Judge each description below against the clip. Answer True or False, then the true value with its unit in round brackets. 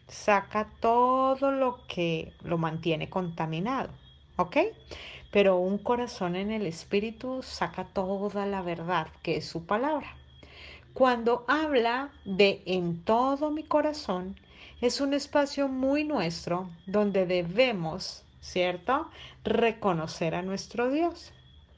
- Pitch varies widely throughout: True (6.5 semitones)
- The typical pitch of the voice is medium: False (200 Hz)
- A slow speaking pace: True (115 wpm)